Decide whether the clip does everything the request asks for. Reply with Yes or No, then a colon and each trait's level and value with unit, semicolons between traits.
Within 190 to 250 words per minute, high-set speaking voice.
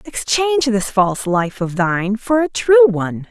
No: average, 180 wpm; high, 230 Hz